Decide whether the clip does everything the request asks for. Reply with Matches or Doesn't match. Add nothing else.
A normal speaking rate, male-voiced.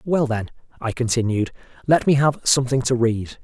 Matches